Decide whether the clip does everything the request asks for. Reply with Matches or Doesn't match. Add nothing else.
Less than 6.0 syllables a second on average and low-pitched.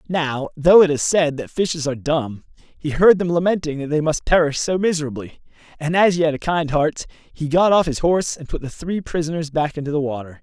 Doesn't match